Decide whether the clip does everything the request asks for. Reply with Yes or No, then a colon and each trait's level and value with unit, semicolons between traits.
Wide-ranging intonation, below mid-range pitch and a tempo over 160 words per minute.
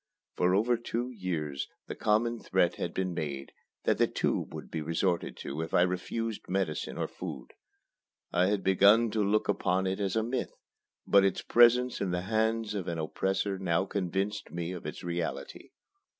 No: average, 3.6 semitones; very low, 95 Hz; average, 180 wpm